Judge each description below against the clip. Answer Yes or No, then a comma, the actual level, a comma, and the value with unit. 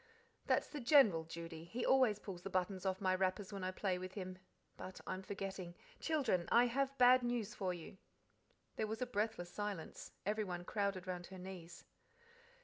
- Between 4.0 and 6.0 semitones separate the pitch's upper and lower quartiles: No, average, 3.3 semitones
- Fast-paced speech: No, average, 175 wpm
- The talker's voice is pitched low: No, high, 190 Hz